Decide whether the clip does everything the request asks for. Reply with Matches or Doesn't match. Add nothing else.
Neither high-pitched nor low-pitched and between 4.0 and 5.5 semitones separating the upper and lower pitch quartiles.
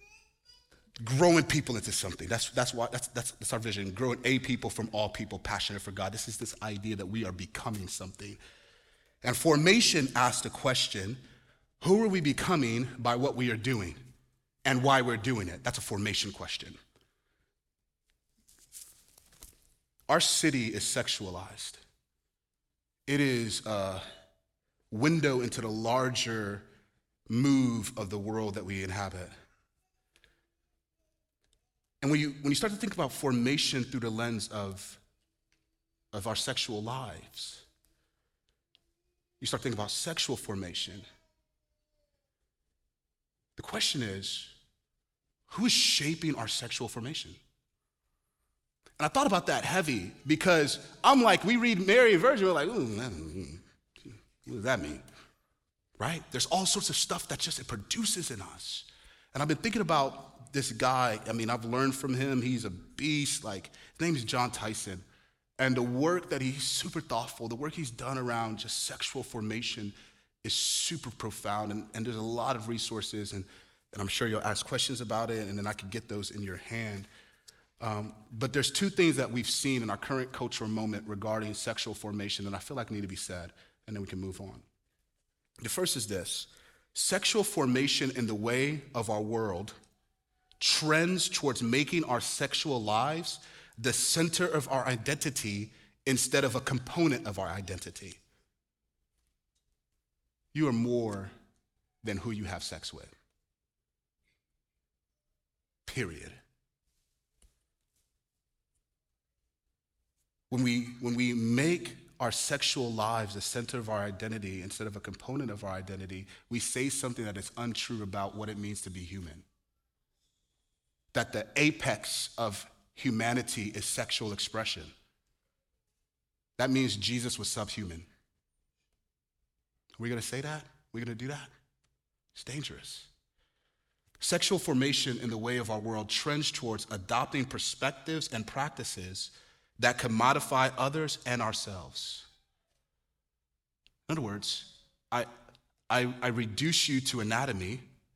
Doesn't match